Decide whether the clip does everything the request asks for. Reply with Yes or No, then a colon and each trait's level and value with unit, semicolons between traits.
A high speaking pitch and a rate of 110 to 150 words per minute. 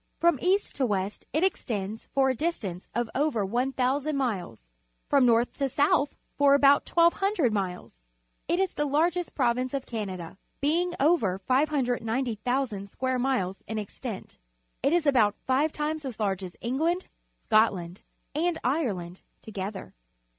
Yes: very high, 255 Hz; average, 140 wpm